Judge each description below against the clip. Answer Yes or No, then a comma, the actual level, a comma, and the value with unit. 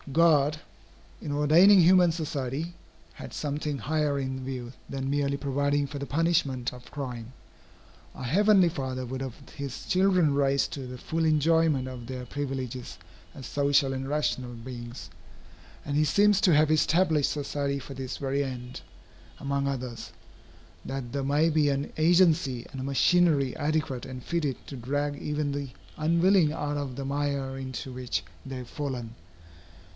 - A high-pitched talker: No, medium, 140 Hz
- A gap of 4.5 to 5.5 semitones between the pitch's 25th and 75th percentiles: No, average, 2.7 semitones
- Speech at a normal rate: Yes, average, 155 wpm